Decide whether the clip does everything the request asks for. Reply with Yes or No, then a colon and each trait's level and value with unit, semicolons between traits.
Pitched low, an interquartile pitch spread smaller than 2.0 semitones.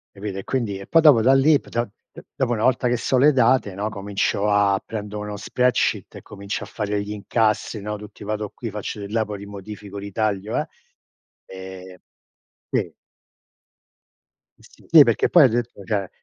No: low, 105 Hz; average, 2.8 semitones